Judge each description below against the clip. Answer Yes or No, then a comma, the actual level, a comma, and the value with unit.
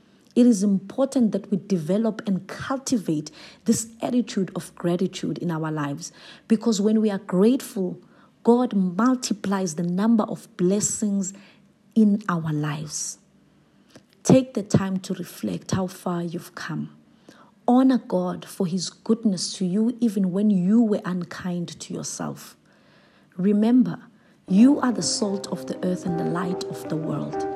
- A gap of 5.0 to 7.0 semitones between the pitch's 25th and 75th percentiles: No, average, 3.9 semitones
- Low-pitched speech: No, high, 195 Hz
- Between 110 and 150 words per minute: Yes, average, 145 wpm